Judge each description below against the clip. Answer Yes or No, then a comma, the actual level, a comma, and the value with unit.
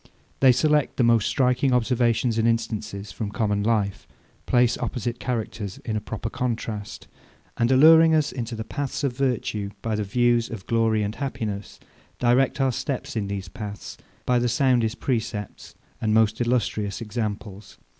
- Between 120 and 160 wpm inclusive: Yes, average, 155 wpm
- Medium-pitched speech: No, low, 115 Hz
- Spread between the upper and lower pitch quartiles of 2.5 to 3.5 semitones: Yes, average, 3.0 semitones